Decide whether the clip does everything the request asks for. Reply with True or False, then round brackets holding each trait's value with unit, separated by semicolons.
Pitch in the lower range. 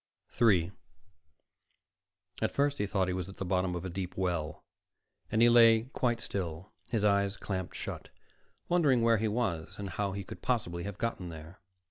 True (100 Hz)